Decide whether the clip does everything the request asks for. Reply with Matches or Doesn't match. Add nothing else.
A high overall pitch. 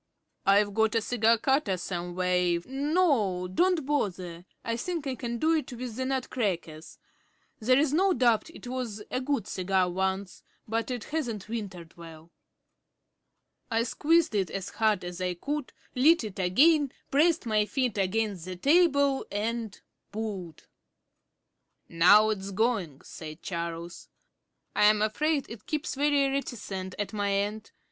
Matches